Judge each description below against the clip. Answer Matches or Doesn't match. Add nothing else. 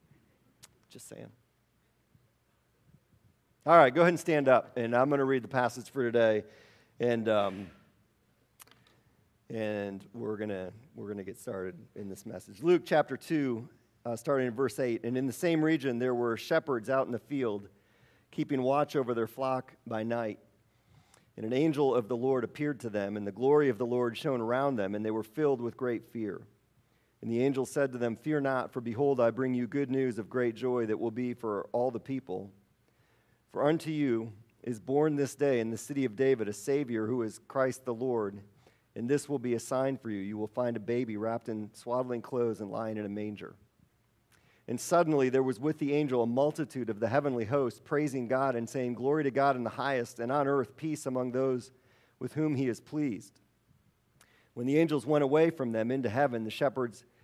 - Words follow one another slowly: Doesn't match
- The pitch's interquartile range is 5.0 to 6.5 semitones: Doesn't match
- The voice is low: Matches